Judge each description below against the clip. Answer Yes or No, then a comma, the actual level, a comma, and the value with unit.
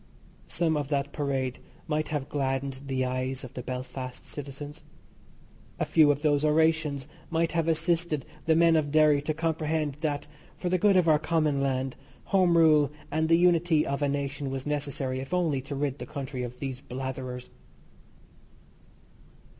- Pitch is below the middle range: No, medium, 145 Hz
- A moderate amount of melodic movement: Yes, average, 3.1 semitones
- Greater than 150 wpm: Yes, average, 165 wpm